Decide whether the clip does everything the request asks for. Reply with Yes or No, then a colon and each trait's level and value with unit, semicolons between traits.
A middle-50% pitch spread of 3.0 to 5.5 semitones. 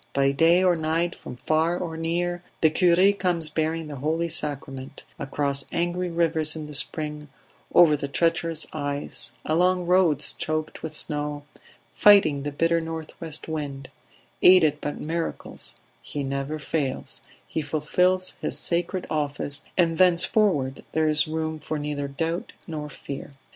No: narrow, 2.5 semitones